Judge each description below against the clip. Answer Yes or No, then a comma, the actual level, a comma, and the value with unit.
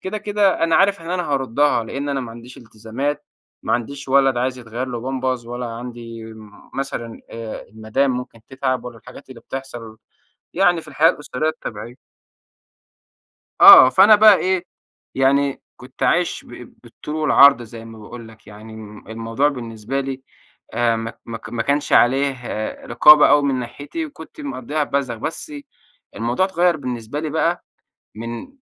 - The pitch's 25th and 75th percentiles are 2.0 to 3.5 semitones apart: No, average, 4.1 semitones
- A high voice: No, low, 130 Hz